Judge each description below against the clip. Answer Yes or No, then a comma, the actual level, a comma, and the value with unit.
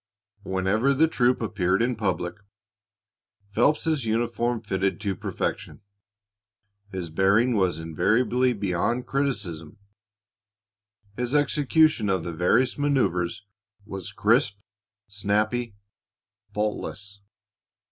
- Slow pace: Yes, slow, 90 wpm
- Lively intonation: No, average, 4.5 semitones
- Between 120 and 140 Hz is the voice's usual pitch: No, low, 105 Hz